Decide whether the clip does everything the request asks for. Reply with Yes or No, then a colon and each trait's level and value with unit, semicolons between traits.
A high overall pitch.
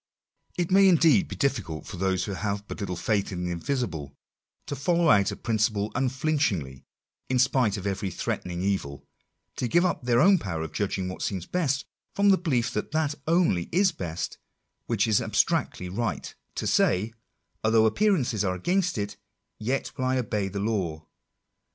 No: low, 110 Hz